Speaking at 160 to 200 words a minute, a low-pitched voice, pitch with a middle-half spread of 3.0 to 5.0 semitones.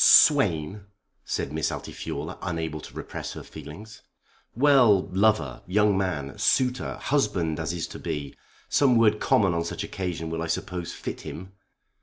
No: average, 150 wpm; very low, 90 Hz; average, 4.7 semitones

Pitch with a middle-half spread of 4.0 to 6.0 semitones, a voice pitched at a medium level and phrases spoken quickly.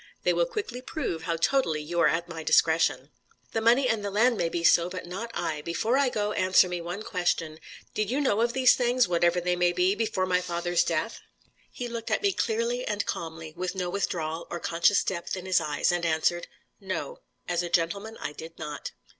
Yes: average, 5.0 semitones; medium, 180 Hz; fast, 215 wpm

